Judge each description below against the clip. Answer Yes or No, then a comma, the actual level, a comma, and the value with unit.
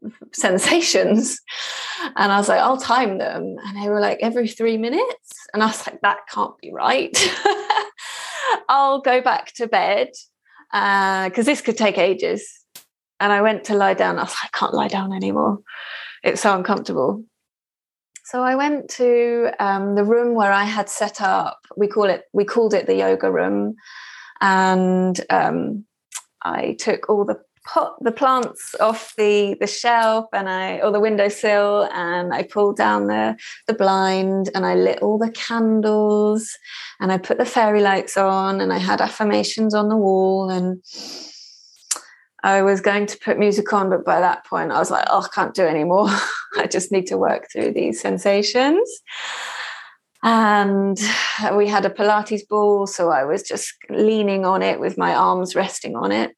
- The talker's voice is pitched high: Yes, high, 210 Hz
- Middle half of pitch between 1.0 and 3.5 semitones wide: Yes, average, 3.1 semitones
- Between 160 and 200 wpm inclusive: Yes, average, 175 wpm